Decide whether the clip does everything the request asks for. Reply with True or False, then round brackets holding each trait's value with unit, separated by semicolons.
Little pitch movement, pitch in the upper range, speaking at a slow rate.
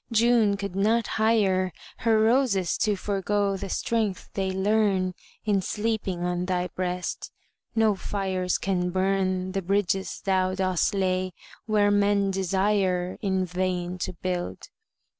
True (1.9 semitones; 195 Hz; 130 wpm)